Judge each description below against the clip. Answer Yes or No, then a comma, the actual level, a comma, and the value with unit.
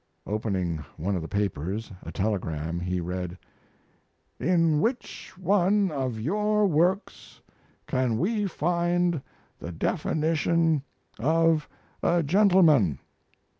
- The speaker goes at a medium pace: No, slow, 100 wpm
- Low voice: No, medium, 150 Hz